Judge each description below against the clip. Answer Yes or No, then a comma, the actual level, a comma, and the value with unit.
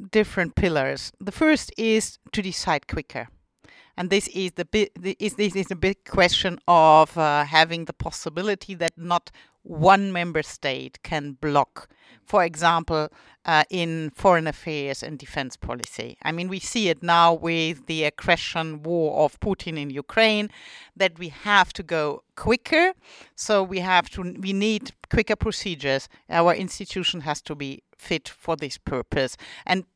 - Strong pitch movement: No, average, 3.8 semitones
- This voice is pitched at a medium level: Yes, medium, 170 Hz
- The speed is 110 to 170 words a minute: Yes, average, 160 wpm